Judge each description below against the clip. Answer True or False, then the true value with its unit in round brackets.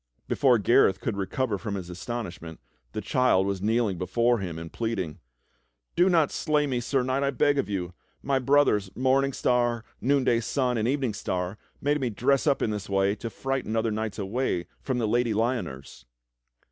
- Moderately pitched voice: False (115 Hz)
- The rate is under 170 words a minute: False (185 wpm)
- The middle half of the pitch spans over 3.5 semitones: True (4.9 semitones)